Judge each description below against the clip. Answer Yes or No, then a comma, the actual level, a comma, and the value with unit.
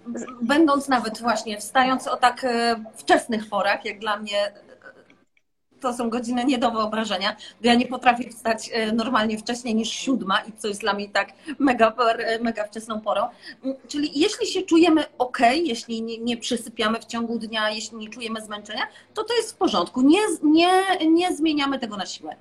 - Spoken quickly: Yes, fast, 170 wpm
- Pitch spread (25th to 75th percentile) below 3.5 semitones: No, average, 4.1 semitones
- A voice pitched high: Yes, high, 235 Hz